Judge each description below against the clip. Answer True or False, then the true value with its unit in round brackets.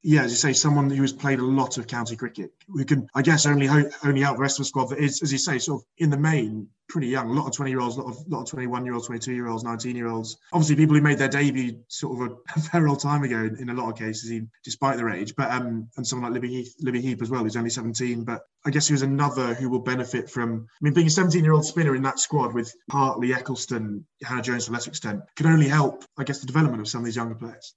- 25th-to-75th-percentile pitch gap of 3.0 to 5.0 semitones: True (3.3 semitones)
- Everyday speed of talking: False (270 wpm)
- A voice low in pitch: True (130 Hz)